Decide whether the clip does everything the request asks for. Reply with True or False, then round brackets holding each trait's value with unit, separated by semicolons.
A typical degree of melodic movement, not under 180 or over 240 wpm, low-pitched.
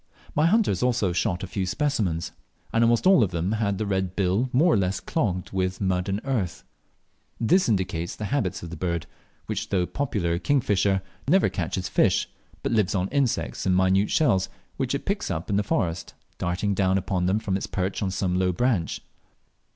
True (4.2 semitones; 195 wpm; 95 Hz)